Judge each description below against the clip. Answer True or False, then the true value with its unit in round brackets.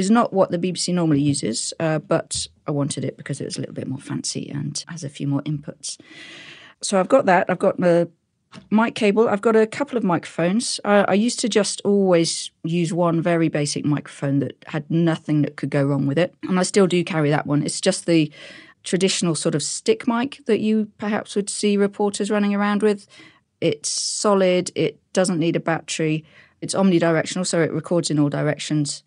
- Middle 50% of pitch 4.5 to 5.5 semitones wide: True (5.0 semitones)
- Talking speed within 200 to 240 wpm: True (205 wpm)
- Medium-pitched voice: True (170 Hz)